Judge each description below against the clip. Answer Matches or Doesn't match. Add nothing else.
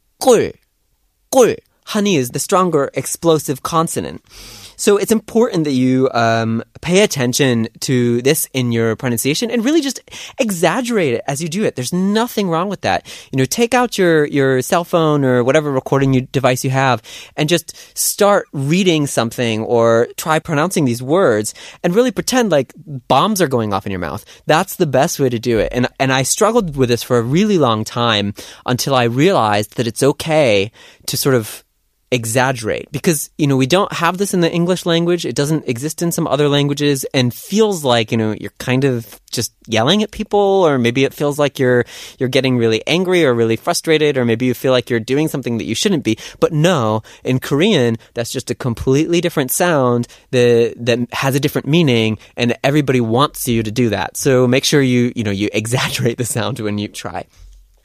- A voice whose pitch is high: Doesn't match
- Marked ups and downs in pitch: Matches